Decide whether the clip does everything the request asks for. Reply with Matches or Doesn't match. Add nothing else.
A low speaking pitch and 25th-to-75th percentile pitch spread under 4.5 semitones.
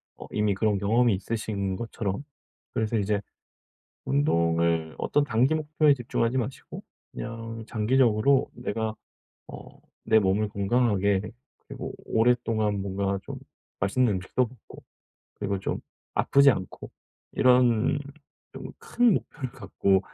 Matches